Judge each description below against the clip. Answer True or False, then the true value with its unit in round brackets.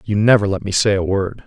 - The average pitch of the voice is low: True (100 Hz)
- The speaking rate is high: True (285 wpm)